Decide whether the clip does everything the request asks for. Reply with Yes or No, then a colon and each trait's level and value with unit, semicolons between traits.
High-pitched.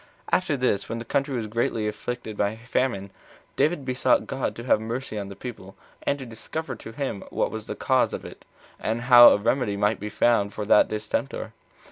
No: low, 115 Hz